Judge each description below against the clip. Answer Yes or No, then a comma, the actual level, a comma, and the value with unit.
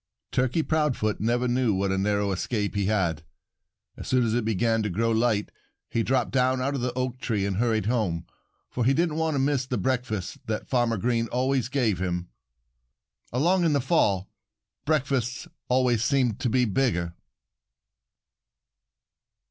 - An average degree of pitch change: Yes, average, 3.6 semitones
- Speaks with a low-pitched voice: Yes, low, 120 Hz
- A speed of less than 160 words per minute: No, average, 165 wpm